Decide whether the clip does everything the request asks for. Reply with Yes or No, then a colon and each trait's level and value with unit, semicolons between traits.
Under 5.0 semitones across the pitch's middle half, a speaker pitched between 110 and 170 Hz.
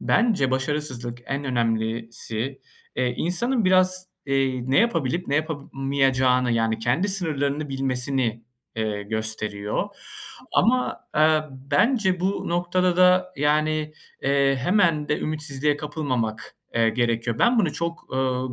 No: wide, 5.4 semitones; medium, 140 Hz